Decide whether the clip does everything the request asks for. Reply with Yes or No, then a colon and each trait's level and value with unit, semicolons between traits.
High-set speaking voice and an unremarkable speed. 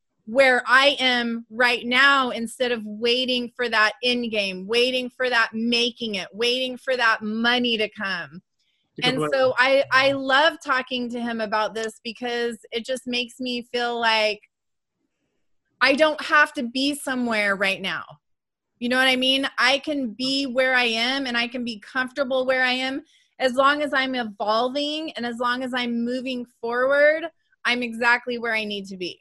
Yes: high, 245 Hz; average, 175 wpm